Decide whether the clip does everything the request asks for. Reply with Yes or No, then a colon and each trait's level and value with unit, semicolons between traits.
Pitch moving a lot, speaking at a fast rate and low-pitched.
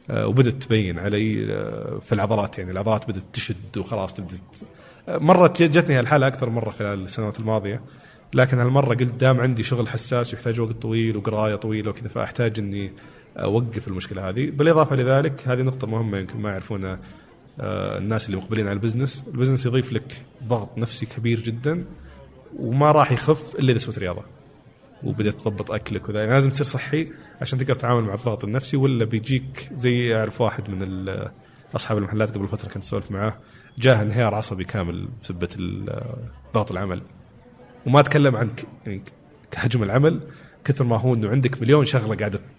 No: average, 3.7 semitones; fast, 160 wpm; low, 115 Hz